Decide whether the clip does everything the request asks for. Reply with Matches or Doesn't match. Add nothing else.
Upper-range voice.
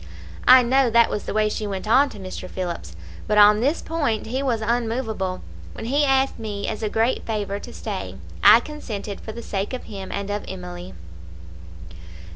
Matches